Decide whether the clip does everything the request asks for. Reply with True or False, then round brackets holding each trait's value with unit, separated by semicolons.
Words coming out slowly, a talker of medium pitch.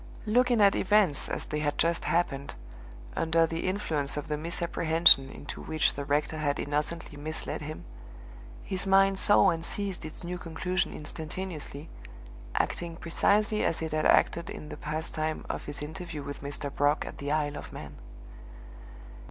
False (160 wpm; 160 Hz)